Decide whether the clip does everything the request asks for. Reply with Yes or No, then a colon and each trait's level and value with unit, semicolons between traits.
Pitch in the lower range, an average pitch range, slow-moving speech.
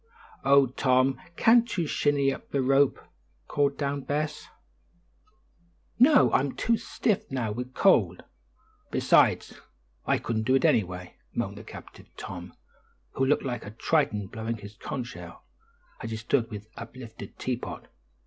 No: low, 130 Hz; average, 4.3 semitones; average, 145 wpm